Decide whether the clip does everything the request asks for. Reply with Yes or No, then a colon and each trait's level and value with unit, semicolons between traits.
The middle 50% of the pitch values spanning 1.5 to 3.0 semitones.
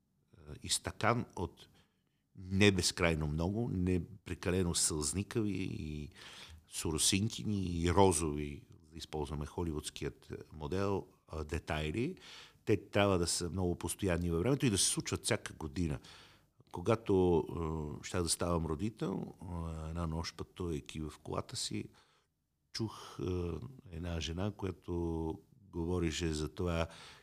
No: average, 3.4 semitones